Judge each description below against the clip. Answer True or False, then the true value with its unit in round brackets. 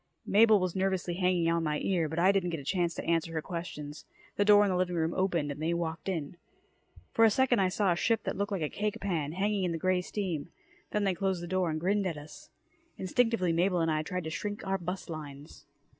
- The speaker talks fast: True (245 wpm)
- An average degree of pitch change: True (3.1 semitones)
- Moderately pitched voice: True (180 Hz)